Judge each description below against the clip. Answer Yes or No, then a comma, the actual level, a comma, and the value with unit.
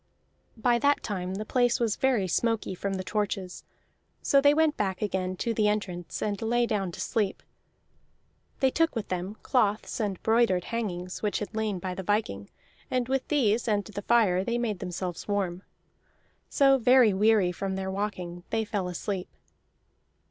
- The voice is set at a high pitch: Yes, high, 210 Hz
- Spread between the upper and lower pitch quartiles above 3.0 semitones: Yes, average, 3.8 semitones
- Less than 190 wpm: Yes, average, 170 wpm